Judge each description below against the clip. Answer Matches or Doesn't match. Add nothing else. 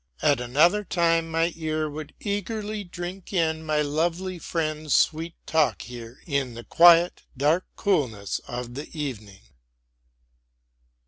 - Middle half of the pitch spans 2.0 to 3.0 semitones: Doesn't match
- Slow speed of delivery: Matches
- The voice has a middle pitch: Matches